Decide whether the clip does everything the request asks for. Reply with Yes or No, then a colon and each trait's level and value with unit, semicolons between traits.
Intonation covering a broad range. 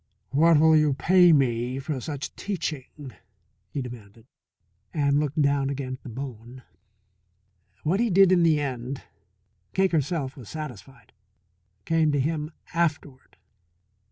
No: average, 3.6 semitones